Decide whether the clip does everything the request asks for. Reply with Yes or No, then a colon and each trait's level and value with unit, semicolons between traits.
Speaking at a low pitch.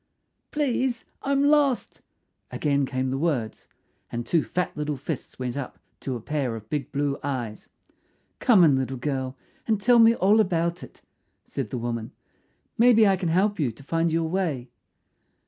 No: medium, 150 Hz